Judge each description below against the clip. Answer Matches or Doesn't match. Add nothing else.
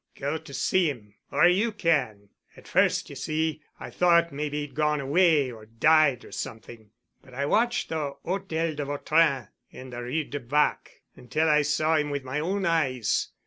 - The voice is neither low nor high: Matches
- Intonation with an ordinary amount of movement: Matches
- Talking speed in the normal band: Matches